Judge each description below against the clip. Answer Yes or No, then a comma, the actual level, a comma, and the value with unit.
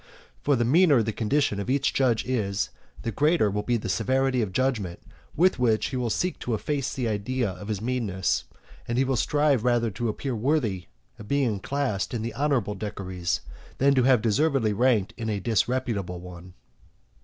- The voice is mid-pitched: No, low, 115 Hz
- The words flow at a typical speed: Yes, average, 185 wpm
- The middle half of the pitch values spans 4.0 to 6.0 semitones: Yes, average, 4.4 semitones